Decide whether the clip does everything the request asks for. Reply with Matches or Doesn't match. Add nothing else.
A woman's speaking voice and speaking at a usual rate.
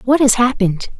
Matches